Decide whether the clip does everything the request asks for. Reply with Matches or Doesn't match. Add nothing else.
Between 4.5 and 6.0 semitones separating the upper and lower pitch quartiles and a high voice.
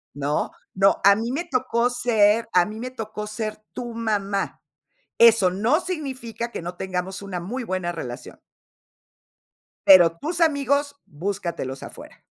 Matches